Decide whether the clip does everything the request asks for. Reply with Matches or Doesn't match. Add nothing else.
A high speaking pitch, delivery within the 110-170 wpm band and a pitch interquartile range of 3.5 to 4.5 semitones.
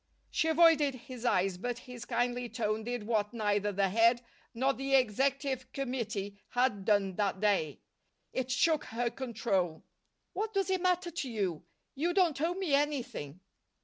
Doesn't match